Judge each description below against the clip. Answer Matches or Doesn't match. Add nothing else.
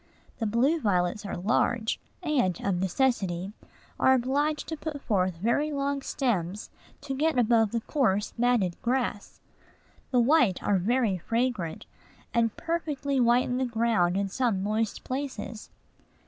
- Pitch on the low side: Doesn't match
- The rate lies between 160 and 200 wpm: Doesn't match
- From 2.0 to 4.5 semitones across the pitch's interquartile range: Doesn't match